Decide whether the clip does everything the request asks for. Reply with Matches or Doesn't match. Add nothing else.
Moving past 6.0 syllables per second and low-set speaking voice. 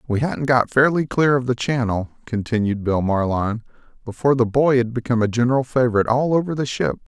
Matches